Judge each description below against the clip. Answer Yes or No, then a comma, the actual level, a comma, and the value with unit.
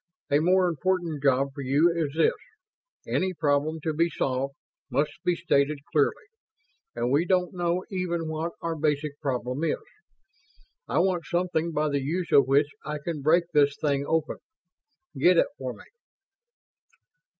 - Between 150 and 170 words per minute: Yes, average, 155 wpm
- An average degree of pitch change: Yes, average, 3.2 semitones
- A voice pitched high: No, medium, 155 Hz